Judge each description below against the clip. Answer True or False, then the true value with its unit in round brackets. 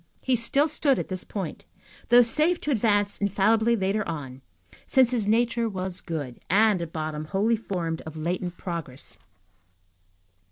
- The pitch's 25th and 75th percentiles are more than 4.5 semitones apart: True (5.6 semitones)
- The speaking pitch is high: True (200 Hz)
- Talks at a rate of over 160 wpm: False (150 wpm)